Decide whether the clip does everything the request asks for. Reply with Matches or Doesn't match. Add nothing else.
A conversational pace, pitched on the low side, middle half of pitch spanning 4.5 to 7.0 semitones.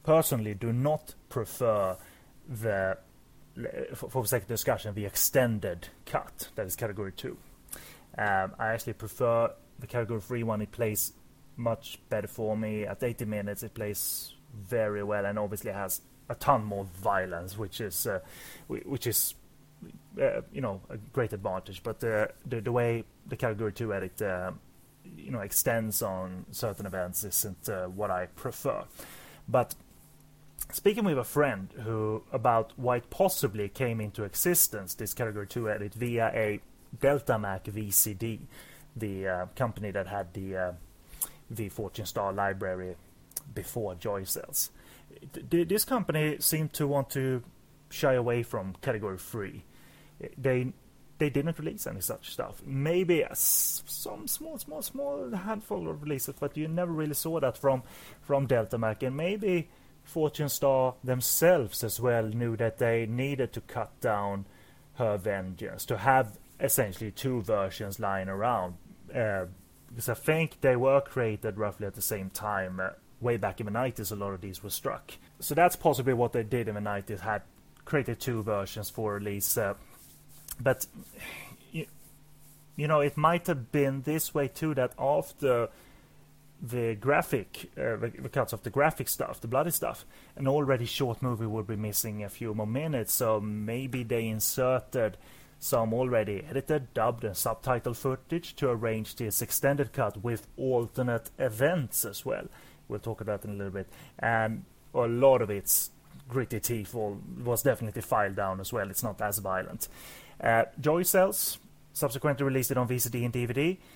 Matches